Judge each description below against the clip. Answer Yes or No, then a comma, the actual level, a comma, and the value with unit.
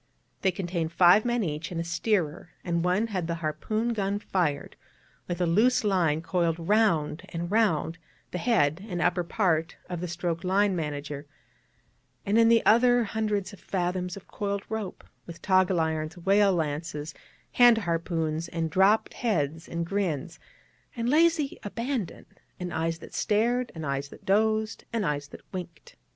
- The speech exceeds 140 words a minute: Yes, average, 160 wpm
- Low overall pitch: No, medium, 180 Hz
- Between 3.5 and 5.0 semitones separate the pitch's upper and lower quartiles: Yes, average, 4.2 semitones